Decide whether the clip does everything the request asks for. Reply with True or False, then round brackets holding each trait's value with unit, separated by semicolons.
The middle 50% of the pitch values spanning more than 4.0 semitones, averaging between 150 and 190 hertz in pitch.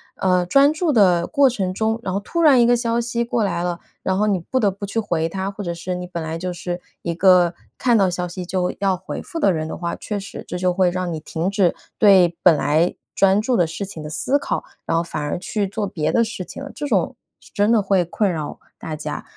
False (3.7 semitones; 185 Hz)